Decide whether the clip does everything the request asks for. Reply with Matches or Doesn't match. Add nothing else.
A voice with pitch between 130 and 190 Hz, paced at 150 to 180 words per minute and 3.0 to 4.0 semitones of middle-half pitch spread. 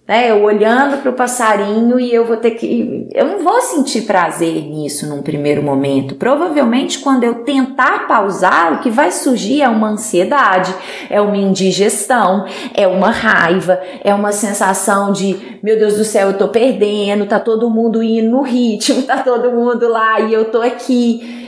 Doesn't match